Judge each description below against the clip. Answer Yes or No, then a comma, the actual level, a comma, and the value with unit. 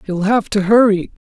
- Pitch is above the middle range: Yes, high, 205 Hz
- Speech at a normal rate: Yes, average, 190 wpm